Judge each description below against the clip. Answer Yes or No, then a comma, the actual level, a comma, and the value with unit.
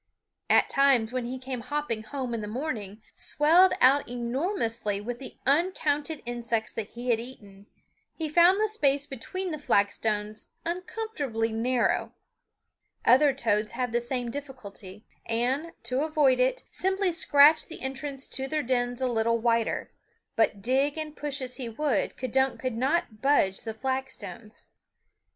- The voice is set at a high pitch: Yes, very high, 255 Hz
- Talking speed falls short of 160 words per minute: Yes, average, 150 wpm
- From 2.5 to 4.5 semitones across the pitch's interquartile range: Yes, average, 4.2 semitones